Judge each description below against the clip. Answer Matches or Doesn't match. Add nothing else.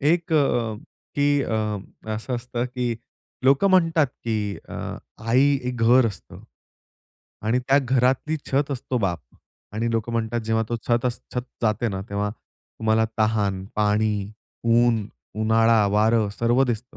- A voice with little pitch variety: Doesn't match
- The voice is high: Doesn't match